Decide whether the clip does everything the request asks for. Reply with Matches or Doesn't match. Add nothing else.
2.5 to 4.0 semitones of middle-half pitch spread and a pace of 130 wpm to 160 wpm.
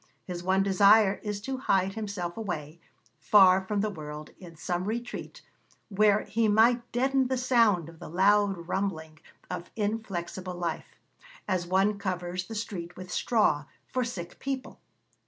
Matches